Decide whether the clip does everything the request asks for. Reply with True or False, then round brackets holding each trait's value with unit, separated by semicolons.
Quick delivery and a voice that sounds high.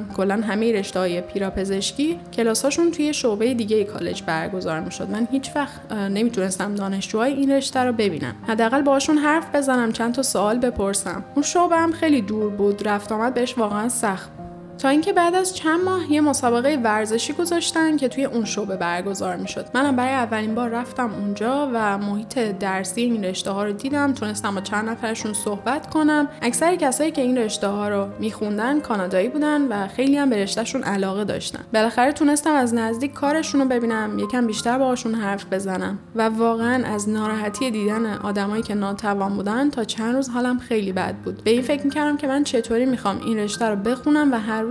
True (185 wpm; 230 Hz)